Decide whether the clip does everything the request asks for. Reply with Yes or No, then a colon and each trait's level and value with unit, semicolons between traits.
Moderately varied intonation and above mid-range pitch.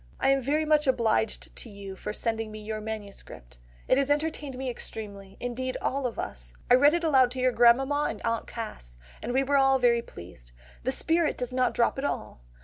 Yes: average, 4.0 semitones; high, 245 Hz